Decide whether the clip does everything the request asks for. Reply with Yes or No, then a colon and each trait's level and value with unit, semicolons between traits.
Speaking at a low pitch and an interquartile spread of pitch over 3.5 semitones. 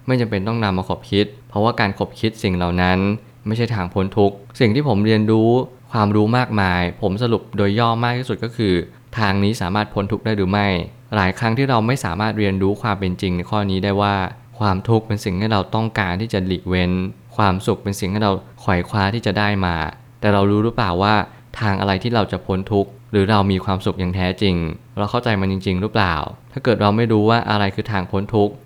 No: low, 105 Hz; average, 2.8 semitones